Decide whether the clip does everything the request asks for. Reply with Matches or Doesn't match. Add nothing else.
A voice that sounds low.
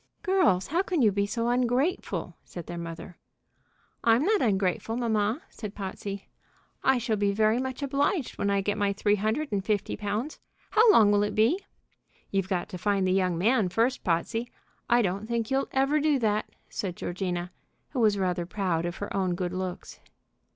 Doesn't match